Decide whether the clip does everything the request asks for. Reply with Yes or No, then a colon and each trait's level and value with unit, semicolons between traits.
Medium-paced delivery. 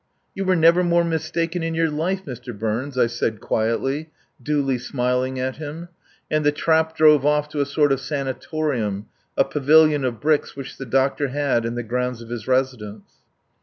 Yes: average, 180 wpm